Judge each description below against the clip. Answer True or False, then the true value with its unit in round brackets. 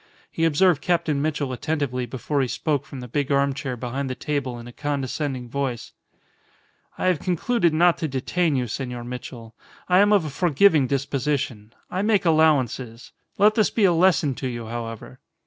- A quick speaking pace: False (175 wpm)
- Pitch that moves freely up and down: False (4.6 semitones)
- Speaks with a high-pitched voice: False (140 Hz)